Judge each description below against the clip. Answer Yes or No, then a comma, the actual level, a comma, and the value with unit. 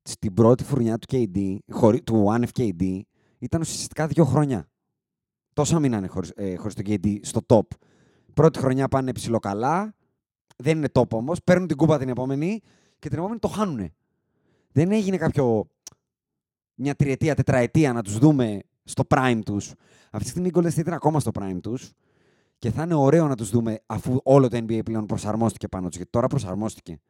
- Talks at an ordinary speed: No, fast, 175 wpm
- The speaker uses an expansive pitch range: Yes, wide, 5.7 semitones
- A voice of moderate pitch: No, low, 125 Hz